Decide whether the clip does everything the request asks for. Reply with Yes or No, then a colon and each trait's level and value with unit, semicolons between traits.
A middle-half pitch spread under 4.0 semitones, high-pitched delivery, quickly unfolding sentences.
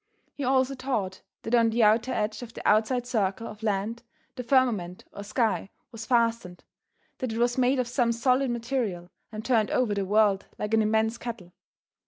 No: average, 2.8 semitones; high, 230 Hz; average, 185 wpm